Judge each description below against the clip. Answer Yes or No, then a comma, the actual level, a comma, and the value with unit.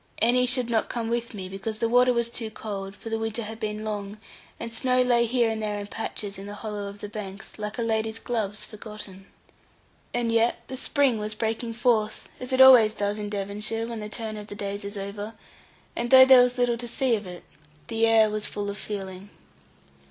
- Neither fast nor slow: No, fast, 220 wpm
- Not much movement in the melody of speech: Yes, narrow, 2.3 semitones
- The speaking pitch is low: No, high, 220 Hz